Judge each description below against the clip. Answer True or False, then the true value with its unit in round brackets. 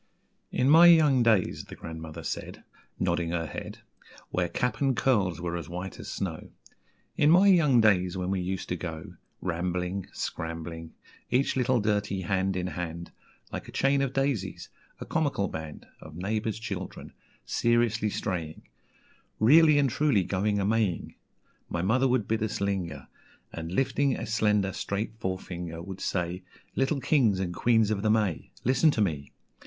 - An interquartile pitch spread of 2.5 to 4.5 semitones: False (5.6 semitones)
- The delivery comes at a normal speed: True (160 wpm)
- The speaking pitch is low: True (100 Hz)